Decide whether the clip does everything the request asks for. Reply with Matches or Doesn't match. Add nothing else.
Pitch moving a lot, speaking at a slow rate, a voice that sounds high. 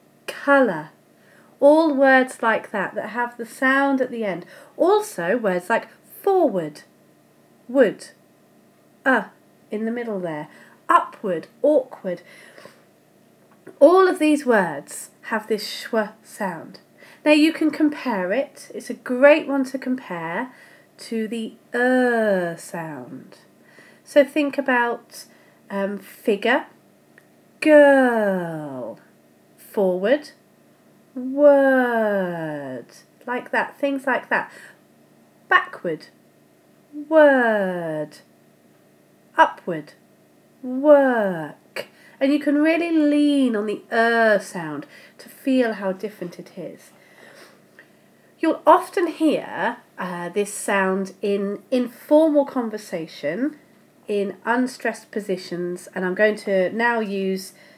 Matches